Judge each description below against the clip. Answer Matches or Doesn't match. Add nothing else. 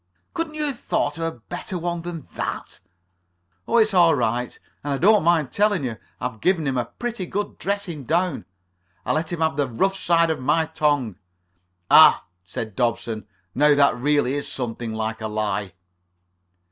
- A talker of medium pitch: Matches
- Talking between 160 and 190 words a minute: Matches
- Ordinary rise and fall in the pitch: Doesn't match